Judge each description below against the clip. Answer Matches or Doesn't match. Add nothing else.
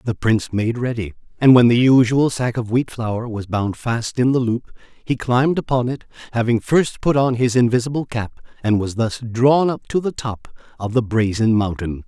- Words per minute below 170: Doesn't match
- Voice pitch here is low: Matches